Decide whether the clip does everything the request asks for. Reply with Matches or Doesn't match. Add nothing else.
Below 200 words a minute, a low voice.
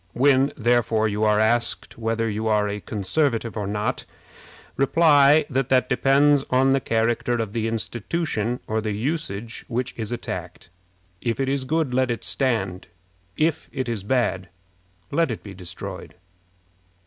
Matches